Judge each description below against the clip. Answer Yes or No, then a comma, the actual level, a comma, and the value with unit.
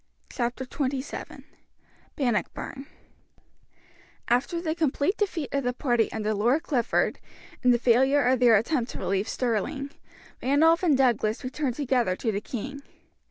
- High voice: Yes, very high, 255 Hz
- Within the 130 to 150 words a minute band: Yes, slow, 135 wpm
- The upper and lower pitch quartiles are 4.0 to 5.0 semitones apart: No, average, 3.2 semitones